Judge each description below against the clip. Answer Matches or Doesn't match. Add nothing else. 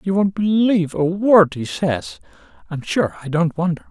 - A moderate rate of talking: Matches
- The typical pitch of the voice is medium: Matches